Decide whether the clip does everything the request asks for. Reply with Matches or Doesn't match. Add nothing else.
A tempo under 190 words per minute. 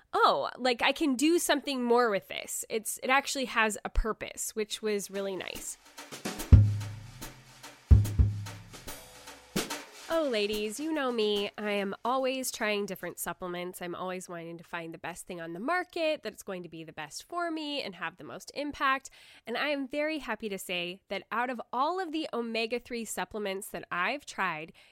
Matches